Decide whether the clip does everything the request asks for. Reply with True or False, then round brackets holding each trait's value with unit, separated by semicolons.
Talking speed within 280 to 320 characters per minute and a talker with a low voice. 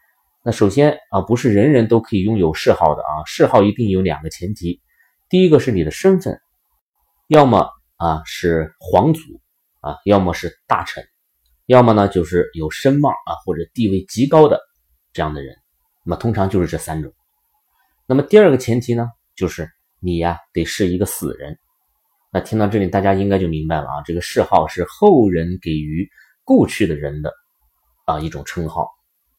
False (260 characters per minute; 95 Hz)